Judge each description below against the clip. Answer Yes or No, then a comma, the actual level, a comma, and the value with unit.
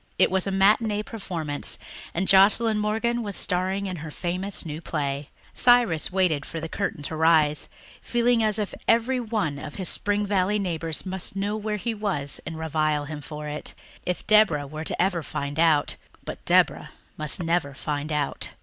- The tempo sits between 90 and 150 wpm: No, average, 175 wpm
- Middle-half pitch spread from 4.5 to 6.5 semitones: Yes, average, 5.2 semitones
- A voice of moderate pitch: Yes, medium, 180 Hz